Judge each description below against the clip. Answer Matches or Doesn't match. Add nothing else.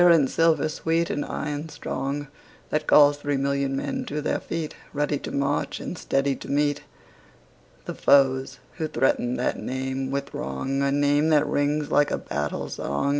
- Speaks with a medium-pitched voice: Matches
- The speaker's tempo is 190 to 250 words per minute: Doesn't match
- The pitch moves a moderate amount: Doesn't match